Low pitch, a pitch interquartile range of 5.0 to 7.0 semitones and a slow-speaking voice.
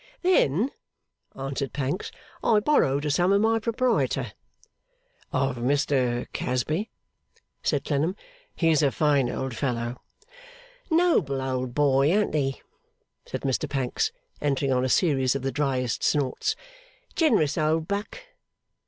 No: medium, 145 Hz; wide, 5.5 semitones; slow, 125 wpm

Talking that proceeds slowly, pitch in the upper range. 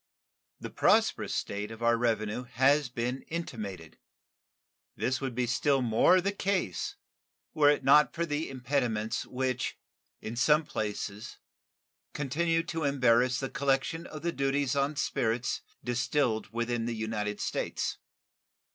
No: slow, 130 wpm; low, 130 Hz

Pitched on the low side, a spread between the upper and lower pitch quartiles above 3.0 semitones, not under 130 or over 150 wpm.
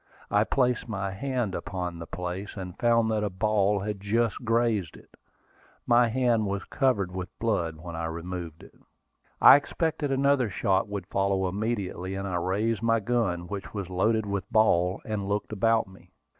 No: low, 100 Hz; average, 3.7 semitones; average, 170 wpm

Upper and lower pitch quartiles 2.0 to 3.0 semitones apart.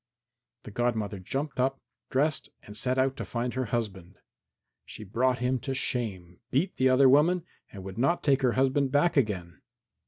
No: average, 4.1 semitones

